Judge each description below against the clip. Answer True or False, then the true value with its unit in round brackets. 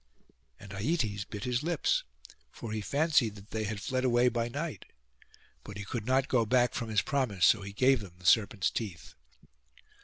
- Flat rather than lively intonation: False (4.1 semitones)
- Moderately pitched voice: False (115 Hz)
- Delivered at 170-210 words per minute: True (185 wpm)